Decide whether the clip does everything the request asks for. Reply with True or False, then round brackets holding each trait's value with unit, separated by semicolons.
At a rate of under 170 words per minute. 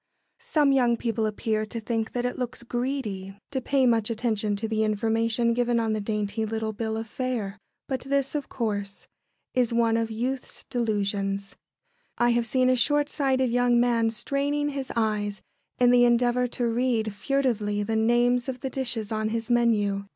False (175 wpm)